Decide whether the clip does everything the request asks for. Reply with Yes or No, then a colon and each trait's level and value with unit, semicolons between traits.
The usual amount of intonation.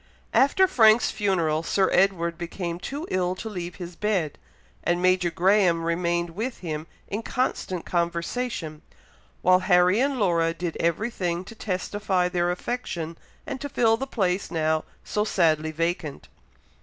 Yes: average, 3.7 semitones